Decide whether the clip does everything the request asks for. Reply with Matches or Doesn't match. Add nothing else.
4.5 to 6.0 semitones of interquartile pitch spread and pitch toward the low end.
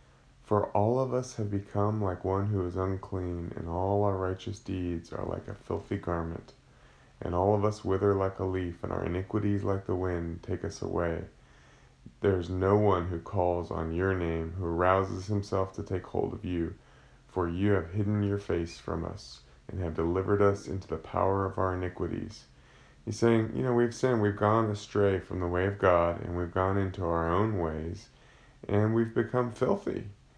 Doesn't match